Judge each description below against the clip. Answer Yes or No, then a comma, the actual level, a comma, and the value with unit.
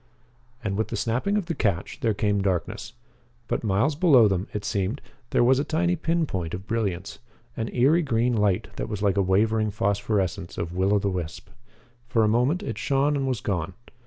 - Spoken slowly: No, average, 200 wpm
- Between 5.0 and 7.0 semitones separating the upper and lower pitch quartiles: Yes, wide, 5.5 semitones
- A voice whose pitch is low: Yes, low, 110 Hz